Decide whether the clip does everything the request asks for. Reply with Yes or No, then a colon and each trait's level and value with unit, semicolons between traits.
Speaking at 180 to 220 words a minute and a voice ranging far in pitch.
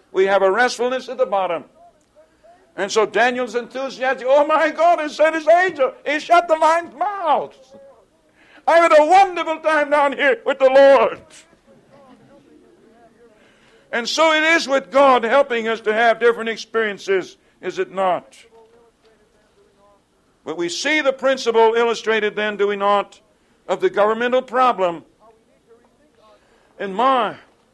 No: average, 140 wpm; wide, 5.8 semitones